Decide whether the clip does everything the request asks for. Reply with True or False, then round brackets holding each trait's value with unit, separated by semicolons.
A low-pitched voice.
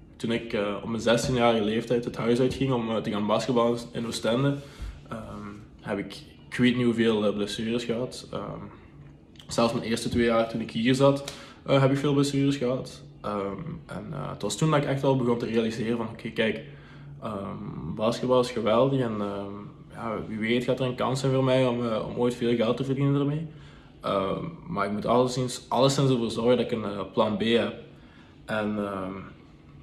True (120 Hz)